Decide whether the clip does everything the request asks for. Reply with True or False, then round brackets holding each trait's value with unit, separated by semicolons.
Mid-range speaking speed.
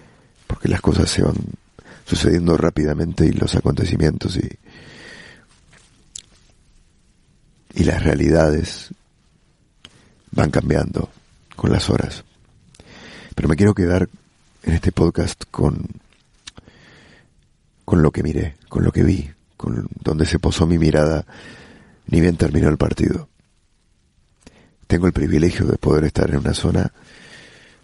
False (120 wpm)